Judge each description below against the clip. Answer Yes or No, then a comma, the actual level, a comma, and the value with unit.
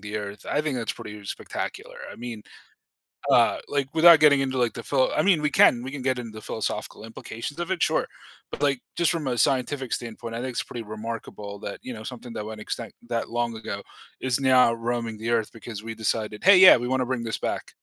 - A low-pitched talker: Yes, low, 120 Hz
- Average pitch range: Yes, average, 3.2 semitones